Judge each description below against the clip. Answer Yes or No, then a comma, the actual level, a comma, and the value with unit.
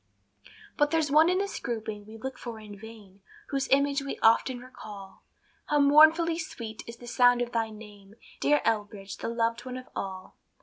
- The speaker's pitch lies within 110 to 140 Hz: No, high, 235 Hz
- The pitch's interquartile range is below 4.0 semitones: No, average, 4.6 semitones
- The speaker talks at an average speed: Yes, average, 180 wpm